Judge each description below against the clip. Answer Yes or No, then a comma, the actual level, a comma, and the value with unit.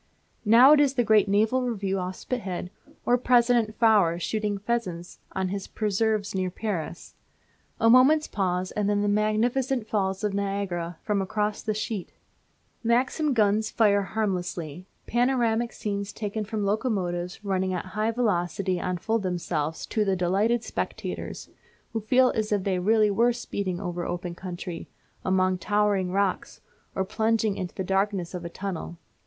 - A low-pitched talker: No, high, 205 Hz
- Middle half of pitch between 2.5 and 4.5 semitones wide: Yes, average, 3.2 semitones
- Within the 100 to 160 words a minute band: Yes, average, 150 wpm